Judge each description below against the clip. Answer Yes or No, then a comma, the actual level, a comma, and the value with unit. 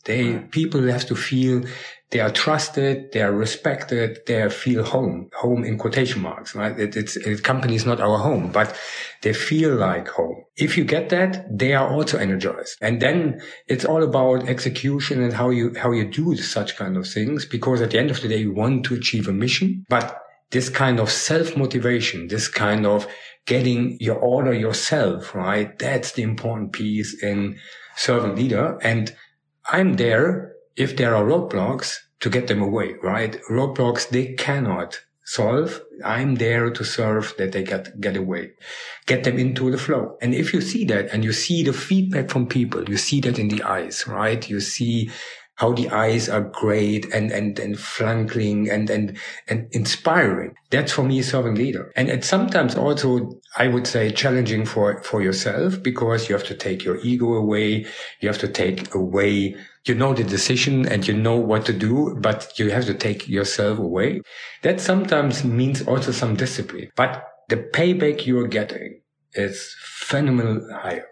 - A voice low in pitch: Yes, low, 120 Hz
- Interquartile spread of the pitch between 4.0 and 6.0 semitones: No, average, 3.5 semitones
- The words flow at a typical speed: Yes, average, 180 wpm